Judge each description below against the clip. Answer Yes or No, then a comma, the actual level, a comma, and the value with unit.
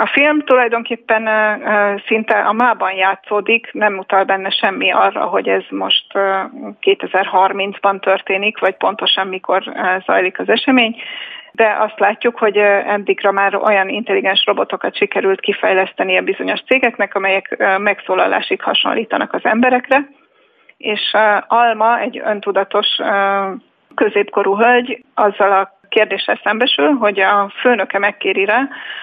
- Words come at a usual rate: Yes, average, 120 wpm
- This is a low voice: No, high, 210 Hz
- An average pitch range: Yes, average, 3.7 semitones